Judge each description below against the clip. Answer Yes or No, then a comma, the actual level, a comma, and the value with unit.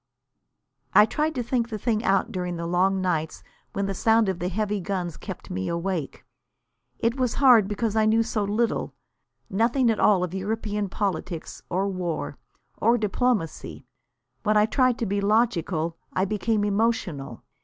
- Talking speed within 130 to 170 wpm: Yes, average, 165 wpm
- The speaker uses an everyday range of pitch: Yes, average, 3.8 semitones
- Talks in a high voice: Yes, high, 205 Hz